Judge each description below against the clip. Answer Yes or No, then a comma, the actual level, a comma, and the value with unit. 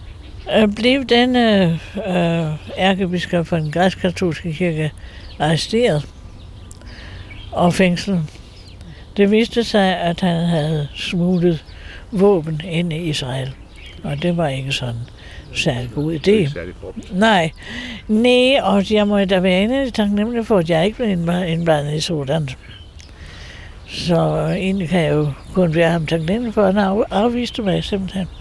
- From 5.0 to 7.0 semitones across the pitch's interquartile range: Yes, wide, 5.5 semitones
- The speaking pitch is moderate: Yes, medium, 170 Hz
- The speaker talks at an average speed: No, slow, 135 wpm